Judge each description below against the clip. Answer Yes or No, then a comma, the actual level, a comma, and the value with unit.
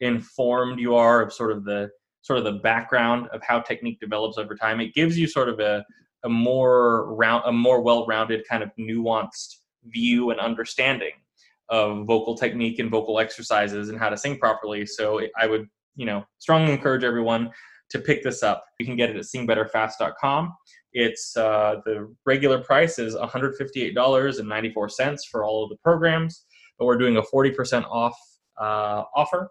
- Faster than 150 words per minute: Yes, average, 175 wpm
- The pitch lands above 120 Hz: No, low, 115 Hz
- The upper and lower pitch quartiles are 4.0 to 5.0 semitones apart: No, narrow, 2.6 semitones